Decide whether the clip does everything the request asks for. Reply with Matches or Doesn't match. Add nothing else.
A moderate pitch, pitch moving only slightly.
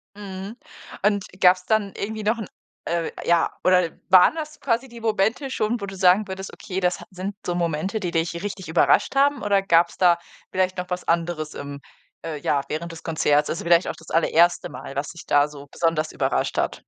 Doesn't match